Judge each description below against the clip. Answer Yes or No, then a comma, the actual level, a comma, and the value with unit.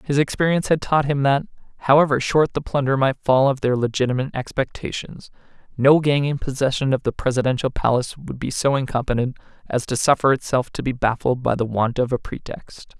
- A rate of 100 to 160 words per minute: No, average, 190 wpm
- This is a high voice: No, low, 135 Hz